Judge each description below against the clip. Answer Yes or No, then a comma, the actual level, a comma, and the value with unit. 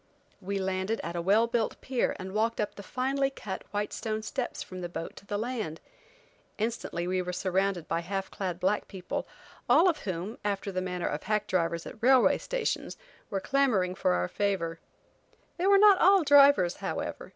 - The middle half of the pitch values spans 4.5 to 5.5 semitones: Yes, average, 4.8 semitones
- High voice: Yes, high, 200 Hz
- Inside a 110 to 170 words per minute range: No, average, 185 wpm